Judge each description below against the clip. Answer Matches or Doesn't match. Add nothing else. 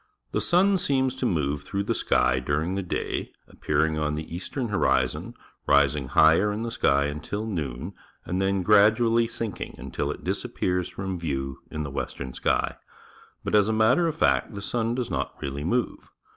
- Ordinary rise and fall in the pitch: Doesn't match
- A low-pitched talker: Matches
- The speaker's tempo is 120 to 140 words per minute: Doesn't match